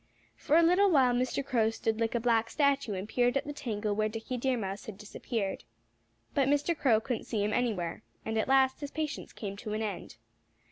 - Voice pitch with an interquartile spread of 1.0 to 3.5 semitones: No, average, 4.1 semitones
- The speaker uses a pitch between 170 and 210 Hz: No, high, 235 Hz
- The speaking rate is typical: No, fast, 215 wpm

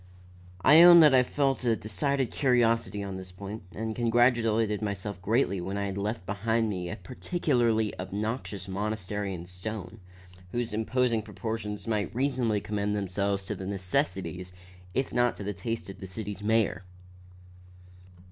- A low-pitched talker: Yes, low, 105 Hz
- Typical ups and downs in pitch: Yes, average, 3.0 semitones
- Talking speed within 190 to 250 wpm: No, average, 150 wpm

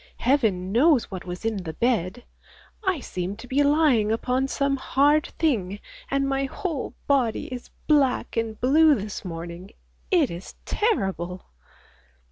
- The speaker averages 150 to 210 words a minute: No, average, 140 wpm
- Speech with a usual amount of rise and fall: No, wide, 6.5 semitones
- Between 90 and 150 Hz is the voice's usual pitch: No, very high, 250 Hz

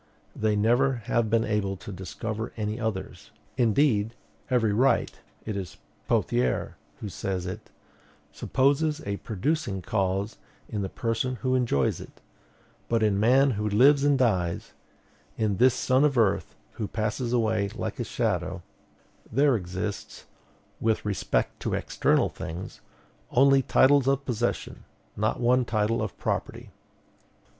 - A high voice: No, low, 110 Hz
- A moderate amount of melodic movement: Yes, average, 4.0 semitones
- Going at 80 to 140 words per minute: Yes, slow, 135 wpm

